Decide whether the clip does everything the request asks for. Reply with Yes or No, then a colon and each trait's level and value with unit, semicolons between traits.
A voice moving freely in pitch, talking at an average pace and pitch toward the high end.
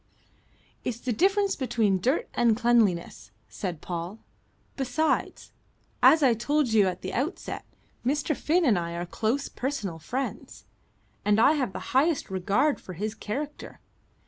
Yes: wide, 6.8 semitones; average, 145 wpm; high, 235 Hz